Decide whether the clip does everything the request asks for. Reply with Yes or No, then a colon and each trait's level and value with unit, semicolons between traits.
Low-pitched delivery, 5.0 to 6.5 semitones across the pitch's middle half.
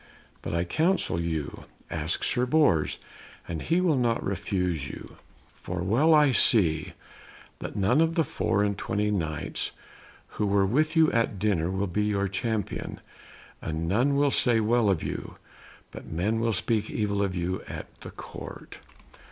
Yes: low, 105 Hz; average, 5.3 semitones